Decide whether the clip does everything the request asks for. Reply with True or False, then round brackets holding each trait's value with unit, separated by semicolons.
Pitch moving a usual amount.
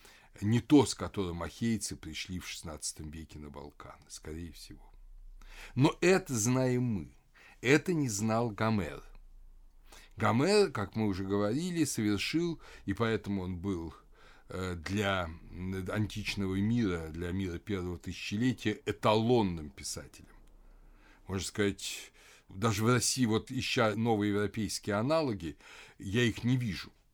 True (4.3 semitones)